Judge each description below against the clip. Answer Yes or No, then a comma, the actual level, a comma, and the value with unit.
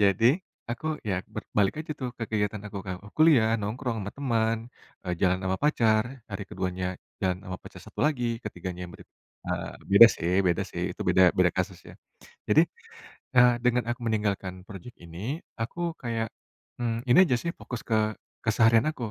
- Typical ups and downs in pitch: Yes, average, 4.3 semitones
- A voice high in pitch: No, low, 110 Hz